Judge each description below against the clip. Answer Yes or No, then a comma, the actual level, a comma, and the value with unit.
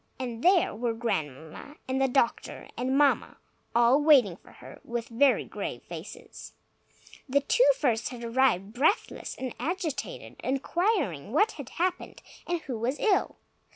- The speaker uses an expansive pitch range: No, average, 4.6 semitones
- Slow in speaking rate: No, average, 145 wpm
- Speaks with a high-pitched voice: Yes, very high, 260 Hz